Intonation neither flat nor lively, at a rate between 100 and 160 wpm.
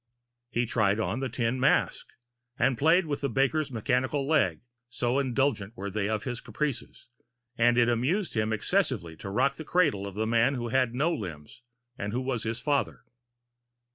No: average, 3.9 semitones; average, 175 wpm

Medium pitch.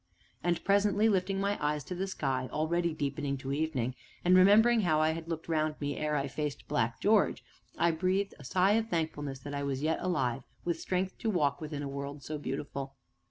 Yes: medium, 155 Hz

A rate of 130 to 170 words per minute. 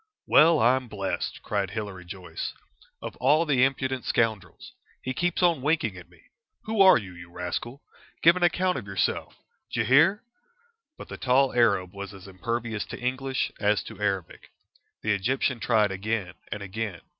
Yes: average, 165 wpm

